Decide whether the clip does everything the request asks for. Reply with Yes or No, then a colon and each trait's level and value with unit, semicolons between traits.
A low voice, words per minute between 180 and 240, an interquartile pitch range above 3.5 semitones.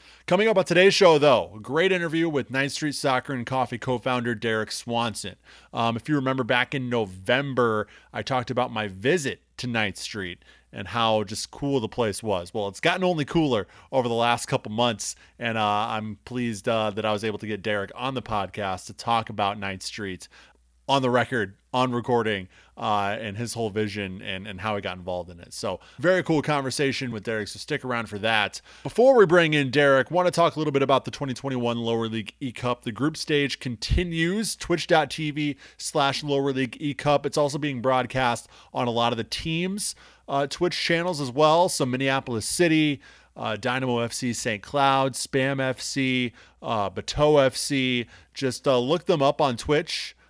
Yes: low, 125 Hz; average, 195 wpm; average, 4.5 semitones